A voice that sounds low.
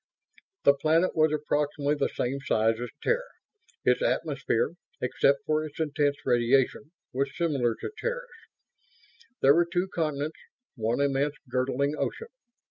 No: medium, 145 Hz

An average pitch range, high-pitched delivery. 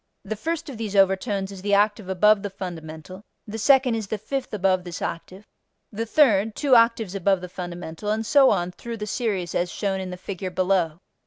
Yes: average, 3.3 semitones; high, 200 Hz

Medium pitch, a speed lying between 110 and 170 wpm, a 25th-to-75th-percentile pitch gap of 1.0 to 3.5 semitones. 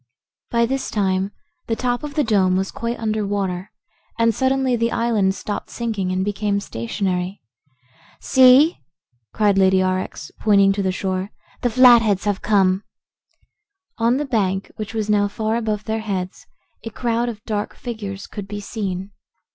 No: high, 210 Hz; average, 155 wpm; average, 3.2 semitones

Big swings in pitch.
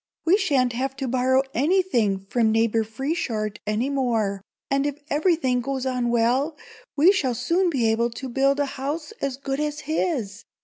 No: average, 3.8 semitones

